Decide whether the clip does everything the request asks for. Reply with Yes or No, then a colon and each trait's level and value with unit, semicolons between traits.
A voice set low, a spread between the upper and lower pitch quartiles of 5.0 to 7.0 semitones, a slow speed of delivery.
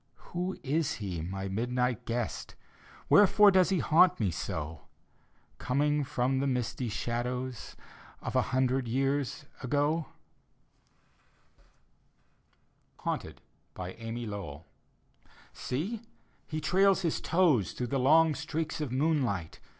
Yes: low, 130 Hz; average, 5.3 semitones; slow, 110 wpm